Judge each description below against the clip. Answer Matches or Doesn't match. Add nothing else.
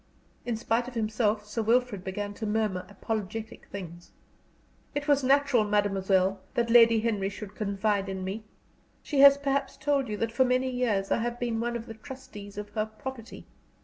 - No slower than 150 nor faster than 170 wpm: Doesn't match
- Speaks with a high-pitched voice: Matches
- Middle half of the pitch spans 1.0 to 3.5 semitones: Matches